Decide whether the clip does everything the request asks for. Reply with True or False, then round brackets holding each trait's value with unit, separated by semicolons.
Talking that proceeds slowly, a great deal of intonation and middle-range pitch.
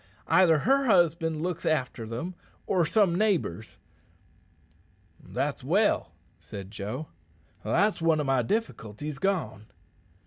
True (110 wpm; 7.7 semitones; 160 Hz)